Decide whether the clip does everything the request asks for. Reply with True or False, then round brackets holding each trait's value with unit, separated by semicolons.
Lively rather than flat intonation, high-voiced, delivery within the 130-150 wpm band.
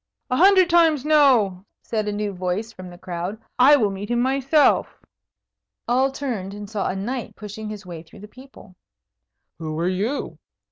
False (5.7 semitones; 215 Hz; 175 wpm)